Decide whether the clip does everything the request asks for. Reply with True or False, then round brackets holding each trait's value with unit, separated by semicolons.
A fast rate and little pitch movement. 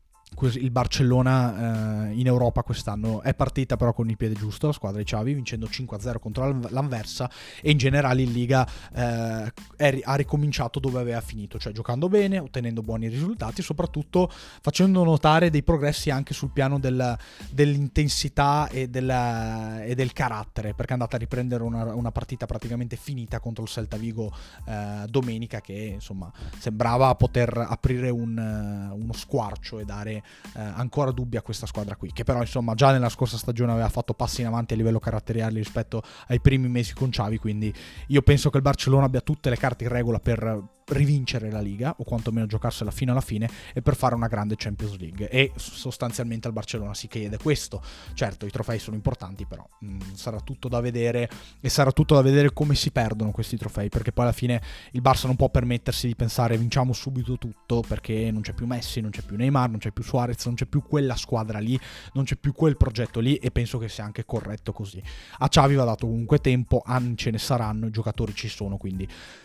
False (195 wpm; 3.0 semitones)